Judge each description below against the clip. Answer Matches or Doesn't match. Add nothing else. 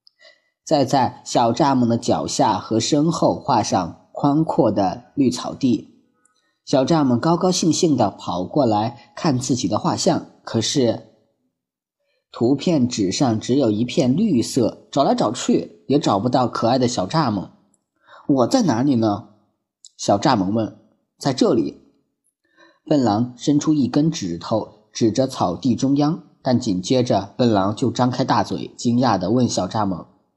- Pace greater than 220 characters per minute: Doesn't match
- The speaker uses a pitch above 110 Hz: Matches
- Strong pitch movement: Doesn't match